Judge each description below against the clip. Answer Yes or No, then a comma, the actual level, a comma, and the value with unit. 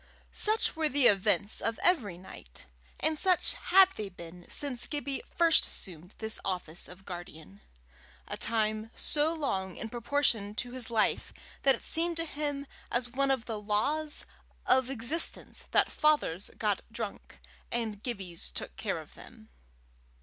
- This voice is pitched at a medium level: No, high, 235 Hz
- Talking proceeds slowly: No, average, 150 wpm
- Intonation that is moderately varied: No, wide, 6.4 semitones